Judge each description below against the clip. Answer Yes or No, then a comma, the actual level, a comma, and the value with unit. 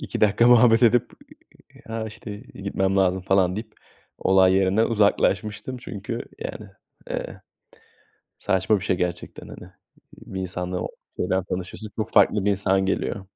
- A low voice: Yes, low, 100 Hz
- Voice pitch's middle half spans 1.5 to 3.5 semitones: Yes, narrow, 2.6 semitones